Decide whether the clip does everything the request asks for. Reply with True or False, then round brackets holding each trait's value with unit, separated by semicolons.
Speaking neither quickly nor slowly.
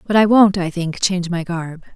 False (245 wpm)